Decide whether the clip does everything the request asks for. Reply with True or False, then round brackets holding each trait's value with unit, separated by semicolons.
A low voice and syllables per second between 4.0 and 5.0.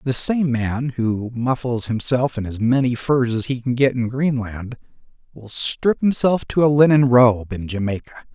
True (125 Hz; 4.4 syllables/s)